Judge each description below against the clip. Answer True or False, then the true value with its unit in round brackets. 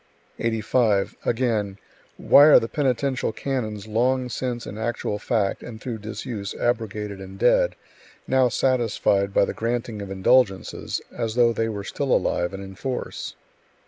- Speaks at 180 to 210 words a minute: False (145 wpm)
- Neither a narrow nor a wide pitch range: True (3.5 semitones)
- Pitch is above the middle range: False (115 Hz)